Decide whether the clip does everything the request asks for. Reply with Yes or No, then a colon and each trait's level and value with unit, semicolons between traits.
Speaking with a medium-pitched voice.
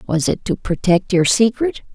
No: high, 205 Hz